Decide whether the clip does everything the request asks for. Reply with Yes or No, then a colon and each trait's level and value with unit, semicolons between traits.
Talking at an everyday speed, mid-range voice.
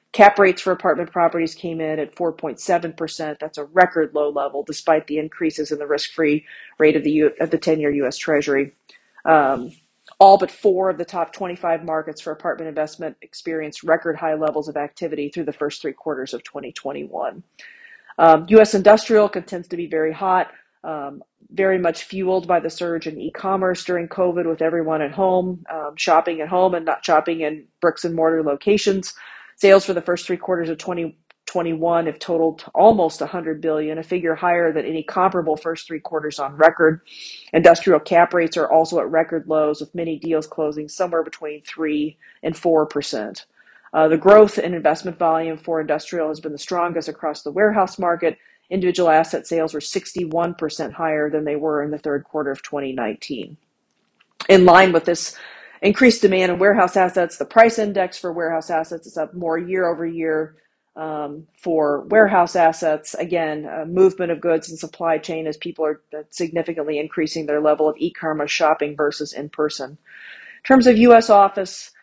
Yes: average, 180 wpm; medium, 165 Hz